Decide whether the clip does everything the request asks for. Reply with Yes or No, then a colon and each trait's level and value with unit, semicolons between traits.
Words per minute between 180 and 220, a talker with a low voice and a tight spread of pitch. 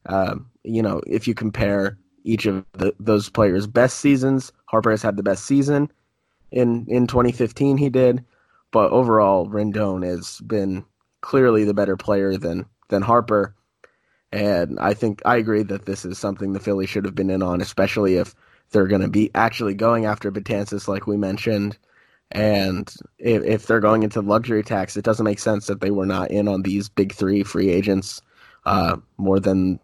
Yes: average, 185 wpm; low, 105 Hz; narrow, 2.3 semitones